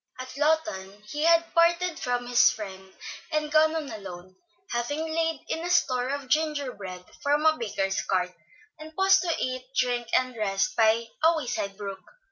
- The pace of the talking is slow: No, average, 165 wpm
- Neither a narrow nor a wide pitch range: No, wide, 7.2 semitones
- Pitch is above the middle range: Yes, very high, 255 Hz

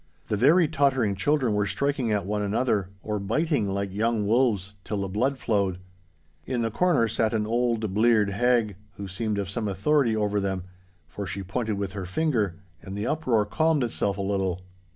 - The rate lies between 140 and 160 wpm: No, average, 185 wpm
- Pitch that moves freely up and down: No, average, 3.7 semitones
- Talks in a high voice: No, low, 105 Hz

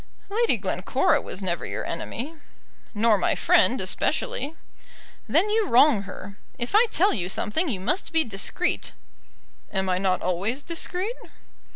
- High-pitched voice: Yes, high, 245 Hz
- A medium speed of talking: Yes, average, 145 wpm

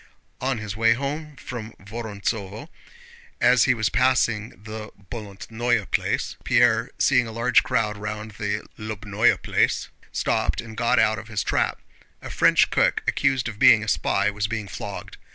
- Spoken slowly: No, average, 155 wpm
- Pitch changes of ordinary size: No, narrow, 2.3 semitones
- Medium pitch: No, low, 110 Hz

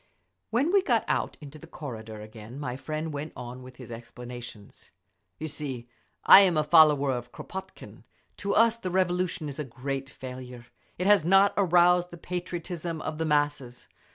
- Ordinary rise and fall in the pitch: No, wide, 5.9 semitones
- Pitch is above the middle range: No, medium, 150 Hz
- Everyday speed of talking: Yes, average, 165 wpm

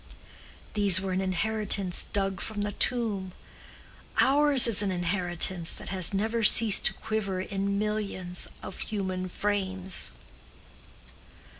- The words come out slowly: Yes, slow, 120 wpm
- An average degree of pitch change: No, narrow, 2.3 semitones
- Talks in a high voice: Yes, high, 195 Hz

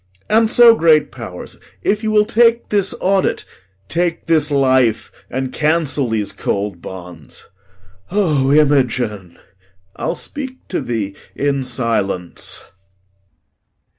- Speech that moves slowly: Yes, slow, 110 wpm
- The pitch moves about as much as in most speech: No, wide, 9.0 semitones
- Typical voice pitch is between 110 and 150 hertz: Yes, medium, 140 Hz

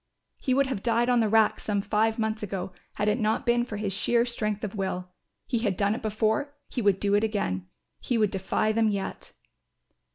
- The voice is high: Yes, high, 215 Hz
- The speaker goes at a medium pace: No, fast, 215 wpm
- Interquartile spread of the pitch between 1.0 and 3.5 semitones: Yes, narrow, 2.4 semitones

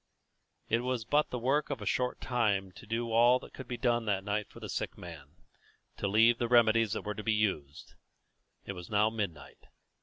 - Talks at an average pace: No, fast, 210 wpm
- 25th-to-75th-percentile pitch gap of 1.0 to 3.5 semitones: Yes, average, 2.9 semitones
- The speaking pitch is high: No, low, 110 Hz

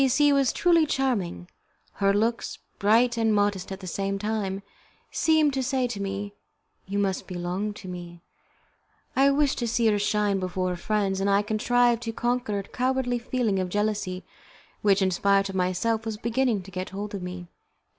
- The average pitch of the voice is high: Yes, high, 205 Hz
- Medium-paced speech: Yes, average, 185 wpm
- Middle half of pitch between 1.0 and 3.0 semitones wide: No, average, 3.9 semitones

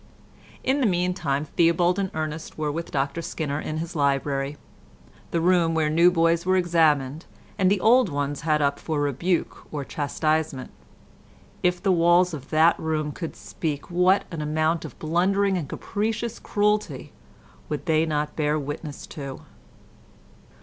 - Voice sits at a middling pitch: Yes, medium, 160 Hz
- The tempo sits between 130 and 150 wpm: Yes, average, 145 wpm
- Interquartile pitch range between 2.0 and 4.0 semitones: Yes, average, 3.1 semitones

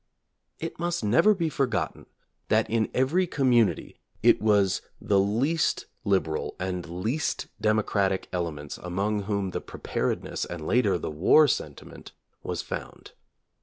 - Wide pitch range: Yes, wide, 5.8 semitones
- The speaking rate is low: Yes, slow, 130 wpm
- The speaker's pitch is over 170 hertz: No, low, 105 Hz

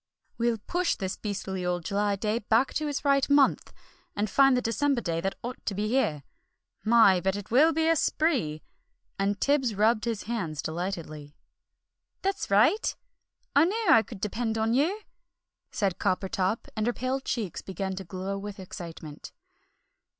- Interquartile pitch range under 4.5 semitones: No, wide, 5.5 semitones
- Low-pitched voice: No, high, 215 Hz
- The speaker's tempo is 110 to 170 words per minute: Yes, average, 165 wpm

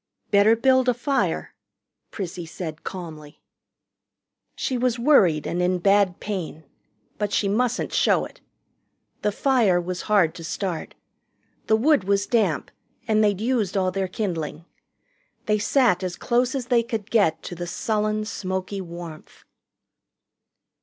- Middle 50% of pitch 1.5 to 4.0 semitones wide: No, average, 4.5 semitones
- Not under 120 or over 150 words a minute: Yes, average, 140 wpm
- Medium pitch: No, high, 200 Hz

